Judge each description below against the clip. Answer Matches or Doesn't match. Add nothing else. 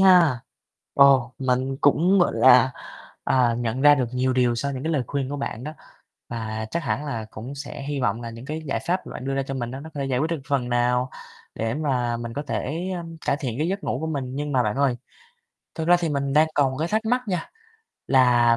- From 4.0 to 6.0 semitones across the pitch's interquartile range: Doesn't match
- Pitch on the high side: Doesn't match